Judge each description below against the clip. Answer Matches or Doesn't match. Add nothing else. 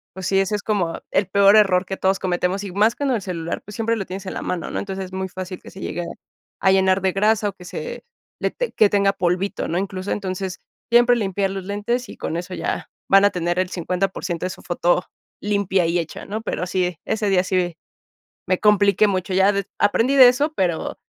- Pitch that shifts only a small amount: Matches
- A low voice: Doesn't match